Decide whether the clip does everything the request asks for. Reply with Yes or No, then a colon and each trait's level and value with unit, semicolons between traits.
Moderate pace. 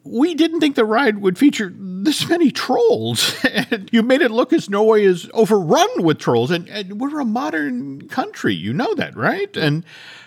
Yes: average, 185 wpm